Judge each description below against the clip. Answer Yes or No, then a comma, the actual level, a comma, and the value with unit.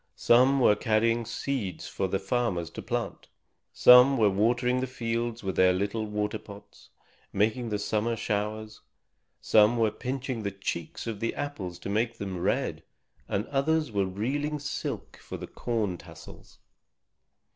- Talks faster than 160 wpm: No, average, 150 wpm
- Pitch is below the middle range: Yes, low, 110 Hz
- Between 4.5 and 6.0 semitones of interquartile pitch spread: No, average, 3.3 semitones